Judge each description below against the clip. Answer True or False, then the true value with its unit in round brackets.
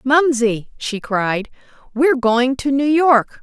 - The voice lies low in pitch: False (255 Hz)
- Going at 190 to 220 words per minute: False (140 wpm)